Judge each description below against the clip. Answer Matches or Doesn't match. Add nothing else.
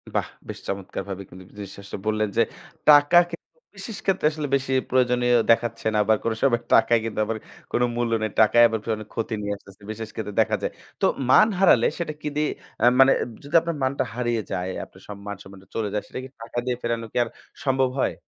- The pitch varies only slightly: Doesn't match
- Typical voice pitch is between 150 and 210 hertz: Doesn't match